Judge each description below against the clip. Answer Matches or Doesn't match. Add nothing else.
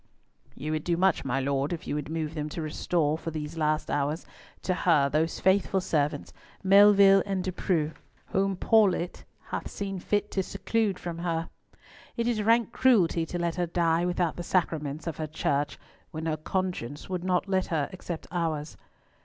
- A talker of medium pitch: Matches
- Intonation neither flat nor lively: Matches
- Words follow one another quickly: Doesn't match